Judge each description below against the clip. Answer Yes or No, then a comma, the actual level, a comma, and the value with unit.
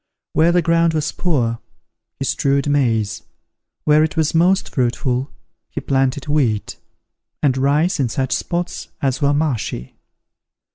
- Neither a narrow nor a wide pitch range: Yes, average, 3.7 semitones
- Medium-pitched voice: Yes, medium, 145 Hz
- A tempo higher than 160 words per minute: No, slow, 135 wpm